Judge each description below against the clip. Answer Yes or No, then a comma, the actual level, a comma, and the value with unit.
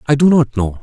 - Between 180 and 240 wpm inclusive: No, fast, 290 wpm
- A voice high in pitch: No, low, 125 Hz